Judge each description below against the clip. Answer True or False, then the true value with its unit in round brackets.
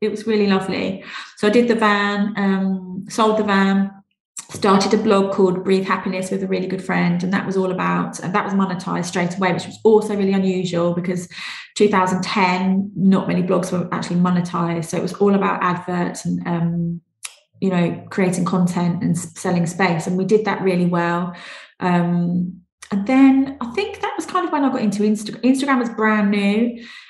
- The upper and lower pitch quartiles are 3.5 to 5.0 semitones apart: False (2.6 semitones)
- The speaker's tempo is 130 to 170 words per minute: False (195 wpm)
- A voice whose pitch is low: False (190 Hz)